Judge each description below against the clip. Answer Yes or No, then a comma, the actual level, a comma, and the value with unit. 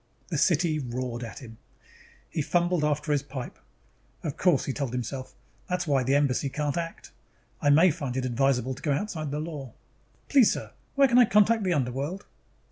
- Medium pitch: Yes, medium, 145 Hz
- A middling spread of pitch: Yes, average, 4.7 semitones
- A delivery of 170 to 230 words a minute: Yes, average, 185 wpm